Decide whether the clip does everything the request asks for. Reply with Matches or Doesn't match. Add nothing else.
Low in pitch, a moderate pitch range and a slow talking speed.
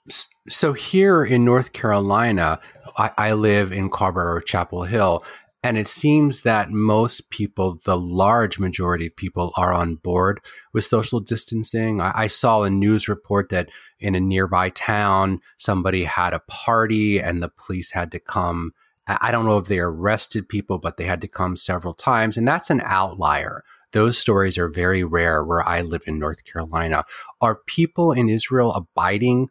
Doesn't match